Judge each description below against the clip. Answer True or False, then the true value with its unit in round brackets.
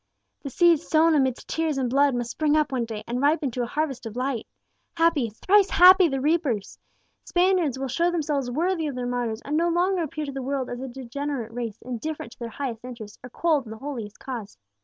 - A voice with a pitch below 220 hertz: False (270 Hz)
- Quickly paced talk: True (220 wpm)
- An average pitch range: True (4.5 semitones)